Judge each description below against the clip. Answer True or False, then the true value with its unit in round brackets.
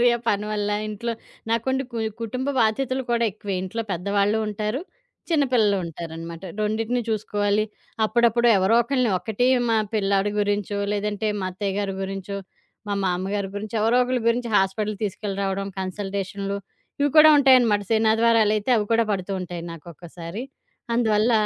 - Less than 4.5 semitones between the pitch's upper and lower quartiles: True (2.8 semitones)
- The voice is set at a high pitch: True (210 Hz)